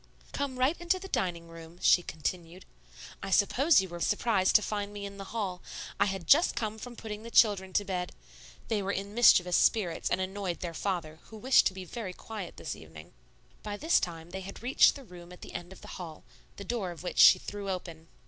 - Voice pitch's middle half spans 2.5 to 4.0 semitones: Yes, average, 3.7 semitones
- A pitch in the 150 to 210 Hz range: Yes, high, 190 Hz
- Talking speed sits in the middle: No, fast, 220 wpm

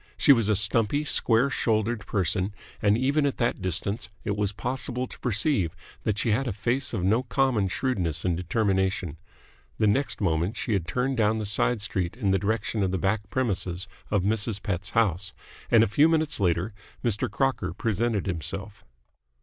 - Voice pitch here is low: Yes, low, 105 Hz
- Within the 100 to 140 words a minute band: No, average, 180 wpm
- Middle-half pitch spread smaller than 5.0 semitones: Yes, average, 3.7 semitones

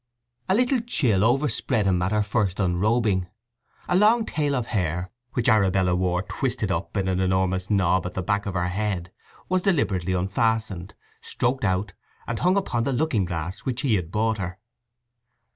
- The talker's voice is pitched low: Yes, low, 100 Hz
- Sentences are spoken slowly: No, average, 175 wpm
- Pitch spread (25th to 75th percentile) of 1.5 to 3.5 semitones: No, average, 4.7 semitones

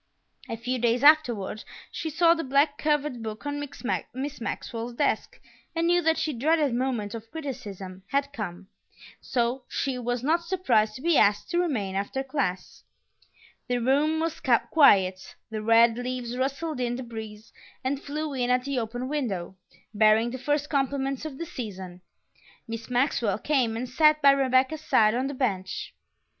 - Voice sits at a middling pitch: No, very high, 255 Hz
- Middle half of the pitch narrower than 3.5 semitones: No, average, 4.4 semitones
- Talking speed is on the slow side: No, average, 165 wpm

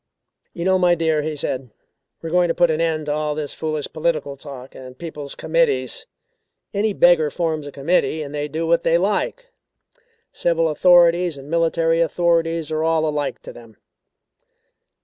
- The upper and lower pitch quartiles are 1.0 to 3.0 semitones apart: Yes, narrow, 2.5 semitones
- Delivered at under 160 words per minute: No, average, 170 wpm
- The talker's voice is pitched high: No, medium, 160 Hz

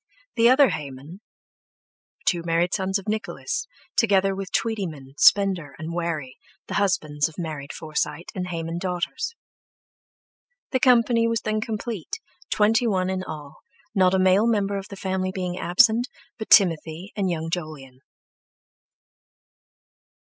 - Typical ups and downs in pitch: Yes, average, 4.6 semitones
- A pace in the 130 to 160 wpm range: Yes, slow, 135 wpm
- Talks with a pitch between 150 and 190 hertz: Yes, medium, 185 Hz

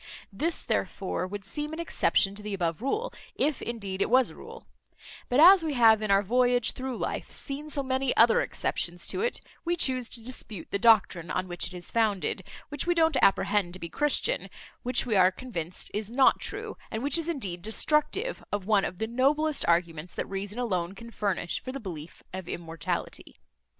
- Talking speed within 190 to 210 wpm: Yes, average, 195 wpm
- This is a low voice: No, high, 225 Hz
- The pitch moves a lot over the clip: Yes, wide, 6.5 semitones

